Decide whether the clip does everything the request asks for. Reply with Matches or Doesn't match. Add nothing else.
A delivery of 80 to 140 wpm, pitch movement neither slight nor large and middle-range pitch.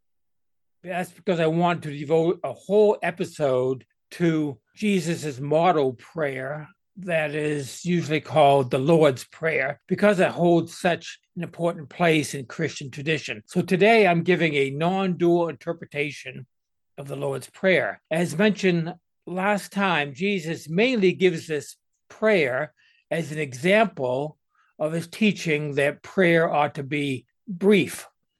Matches